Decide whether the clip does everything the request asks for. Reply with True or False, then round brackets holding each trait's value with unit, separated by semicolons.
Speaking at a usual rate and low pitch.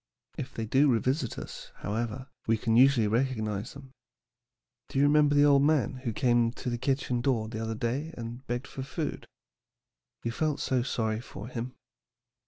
True (175 wpm; 125 Hz)